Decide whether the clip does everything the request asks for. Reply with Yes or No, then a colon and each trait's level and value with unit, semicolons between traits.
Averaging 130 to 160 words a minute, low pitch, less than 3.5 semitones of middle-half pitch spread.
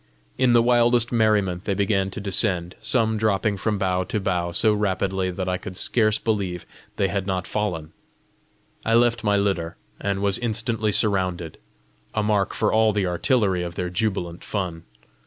No: average, 170 wpm; low, 100 Hz; average, 3.1 semitones